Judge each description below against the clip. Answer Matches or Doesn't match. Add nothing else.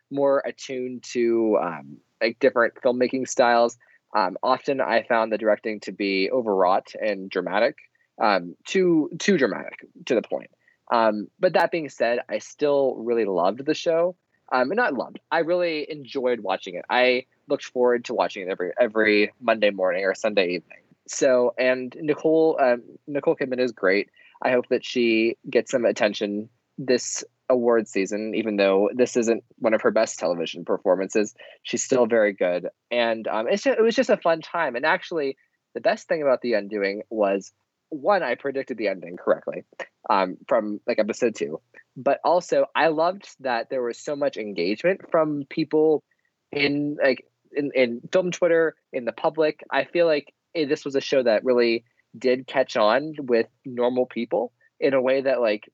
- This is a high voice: Doesn't match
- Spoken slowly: Doesn't match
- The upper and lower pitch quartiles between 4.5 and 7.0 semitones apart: Matches